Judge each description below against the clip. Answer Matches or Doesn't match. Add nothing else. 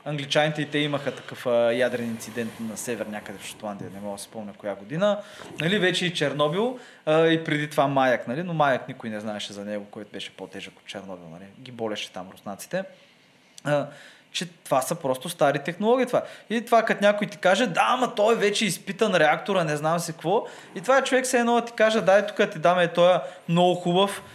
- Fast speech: Matches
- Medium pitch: Matches